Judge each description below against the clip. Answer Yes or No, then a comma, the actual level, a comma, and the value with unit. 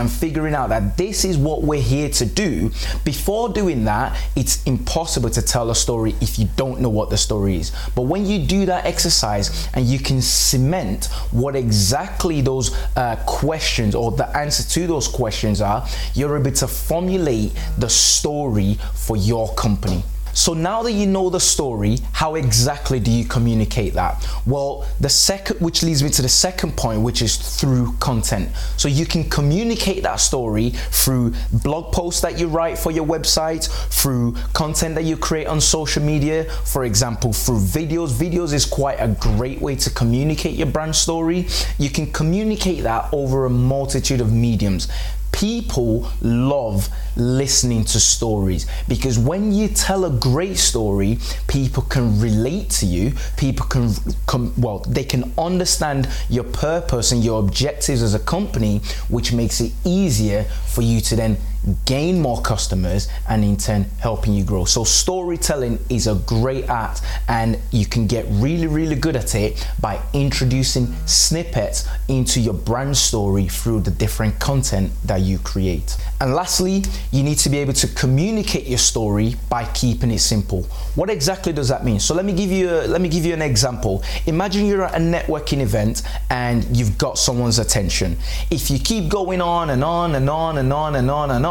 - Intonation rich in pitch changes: Yes, wide, 6.2 semitones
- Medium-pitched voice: No, low, 130 Hz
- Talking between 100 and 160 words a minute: No, average, 175 wpm